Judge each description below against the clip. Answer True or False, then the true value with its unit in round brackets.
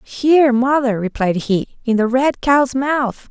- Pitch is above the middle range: True (250 Hz)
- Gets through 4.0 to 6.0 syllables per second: False (3.8 syllables/s)